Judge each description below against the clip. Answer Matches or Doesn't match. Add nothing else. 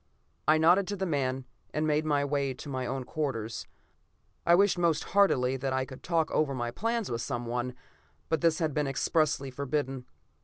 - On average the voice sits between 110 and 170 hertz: Matches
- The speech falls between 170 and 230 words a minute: Matches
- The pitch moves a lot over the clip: Doesn't match